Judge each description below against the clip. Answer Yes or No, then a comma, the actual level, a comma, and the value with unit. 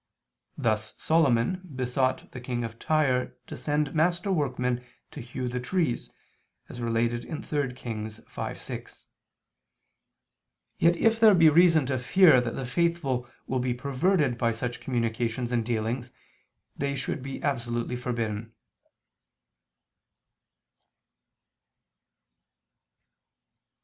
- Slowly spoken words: Yes, slow, 110 wpm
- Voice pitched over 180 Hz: No, low, 125 Hz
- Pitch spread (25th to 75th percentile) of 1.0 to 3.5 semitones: No, average, 4.1 semitones